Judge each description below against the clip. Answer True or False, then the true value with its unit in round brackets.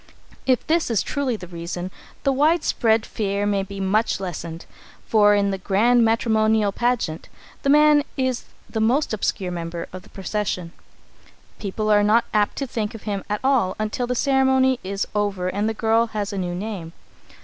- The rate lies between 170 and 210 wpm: True (175 wpm)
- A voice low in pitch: False (215 Hz)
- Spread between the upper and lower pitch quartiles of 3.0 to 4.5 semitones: True (3.8 semitones)